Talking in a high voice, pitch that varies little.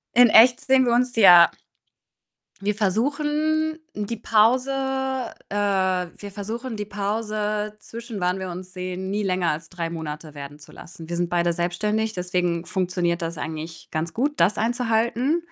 No: high, 200 Hz; average, 4.6 semitones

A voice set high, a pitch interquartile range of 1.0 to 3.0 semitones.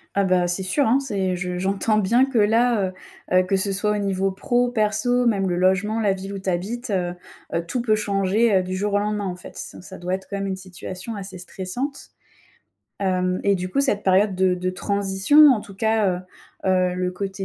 Yes: high, 195 Hz; narrow, 2.5 semitones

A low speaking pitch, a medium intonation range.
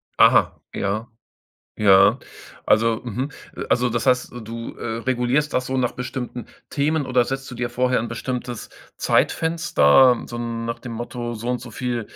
No: low, 120 Hz; narrow, 1.8 semitones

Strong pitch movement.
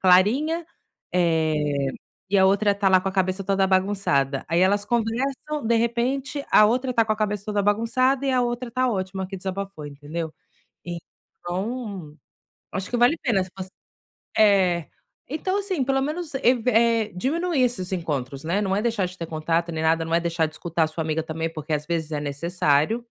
Yes: wide, 6.0 semitones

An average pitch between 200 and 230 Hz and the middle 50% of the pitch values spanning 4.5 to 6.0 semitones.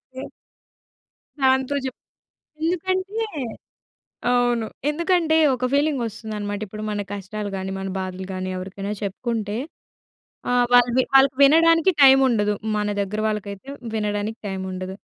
Yes: high, 225 Hz; average, 4.9 semitones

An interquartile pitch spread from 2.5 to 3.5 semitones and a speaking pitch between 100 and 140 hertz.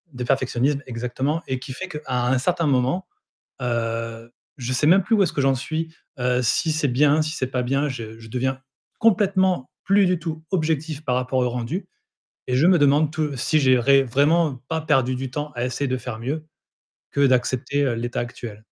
No: average, 4.0 semitones; low, 135 Hz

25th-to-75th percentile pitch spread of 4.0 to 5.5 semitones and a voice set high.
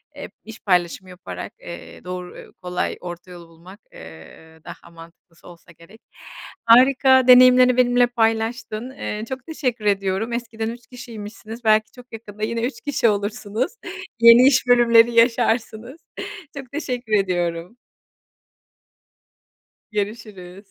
Yes: average, 4.6 semitones; high, 225 Hz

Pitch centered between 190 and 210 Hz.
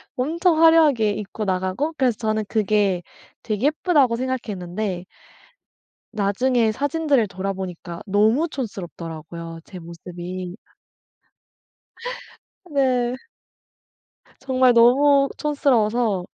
No: high, 220 Hz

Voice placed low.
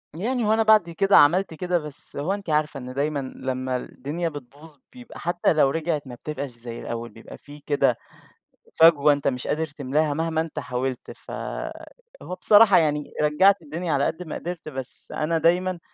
No: medium, 155 Hz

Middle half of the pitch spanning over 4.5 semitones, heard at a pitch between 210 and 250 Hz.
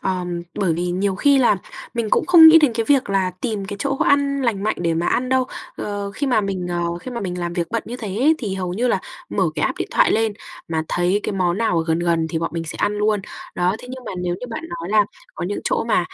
No: wide, 5.6 semitones; high, 200 Hz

